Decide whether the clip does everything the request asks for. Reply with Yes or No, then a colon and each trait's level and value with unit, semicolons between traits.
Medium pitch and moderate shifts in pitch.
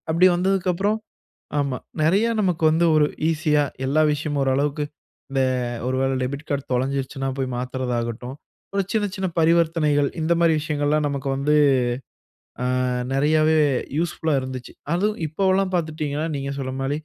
Yes: medium, 150 Hz; average, 3.6 semitones